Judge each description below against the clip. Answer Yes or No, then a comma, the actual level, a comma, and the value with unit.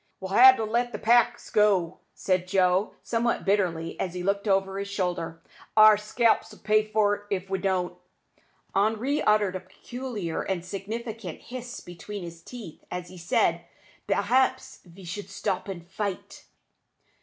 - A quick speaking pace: No, average, 150 wpm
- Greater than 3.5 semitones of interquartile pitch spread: No, average, 3.1 semitones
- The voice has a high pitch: Yes, high, 200 Hz